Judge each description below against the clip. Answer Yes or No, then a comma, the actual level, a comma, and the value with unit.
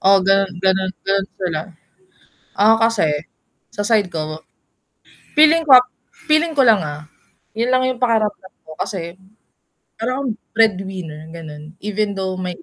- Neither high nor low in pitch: No, high, 195 Hz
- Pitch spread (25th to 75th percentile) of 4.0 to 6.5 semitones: Yes, average, 4.5 semitones